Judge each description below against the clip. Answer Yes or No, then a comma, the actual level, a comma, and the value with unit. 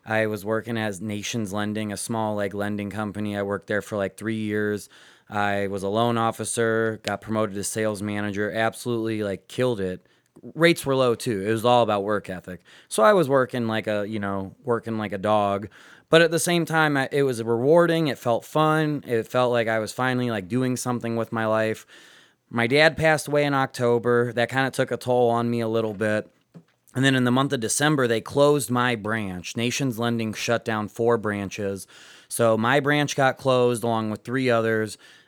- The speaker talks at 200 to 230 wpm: Yes, fast, 205 wpm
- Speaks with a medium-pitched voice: No, low, 115 Hz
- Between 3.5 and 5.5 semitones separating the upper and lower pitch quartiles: No, average, 3.0 semitones